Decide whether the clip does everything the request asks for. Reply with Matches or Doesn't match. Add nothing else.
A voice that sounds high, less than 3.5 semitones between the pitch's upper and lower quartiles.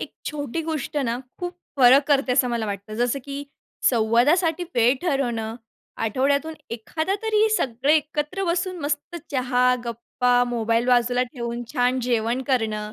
Doesn't match